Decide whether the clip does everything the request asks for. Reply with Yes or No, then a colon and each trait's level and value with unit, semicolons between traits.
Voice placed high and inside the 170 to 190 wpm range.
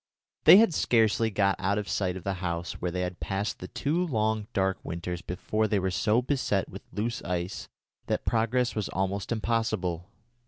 No: low, 100 Hz; average, 185 wpm